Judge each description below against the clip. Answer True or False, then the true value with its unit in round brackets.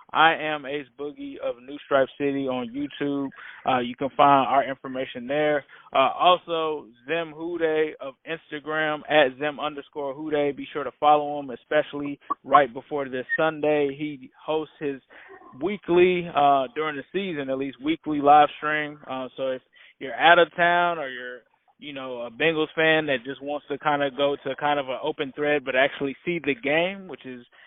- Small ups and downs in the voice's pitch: True (2.2 semitones)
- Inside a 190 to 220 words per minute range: False (180 wpm)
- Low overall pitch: False (145 Hz)